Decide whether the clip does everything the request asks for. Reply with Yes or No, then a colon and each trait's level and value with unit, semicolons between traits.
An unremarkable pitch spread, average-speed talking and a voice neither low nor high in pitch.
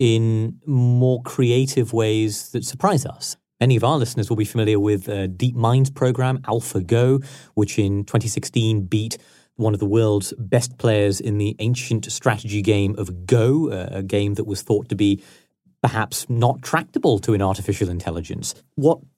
No: average, 3.3 semitones; average, 165 wpm; low, 110 Hz